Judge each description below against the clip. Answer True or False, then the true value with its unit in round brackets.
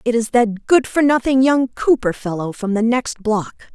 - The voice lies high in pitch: True (235 Hz)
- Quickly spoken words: True (210 wpm)